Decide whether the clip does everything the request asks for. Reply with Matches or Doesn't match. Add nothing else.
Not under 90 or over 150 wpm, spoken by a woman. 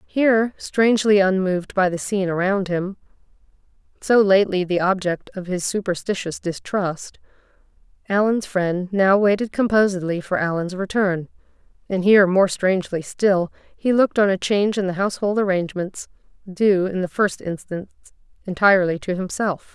Matches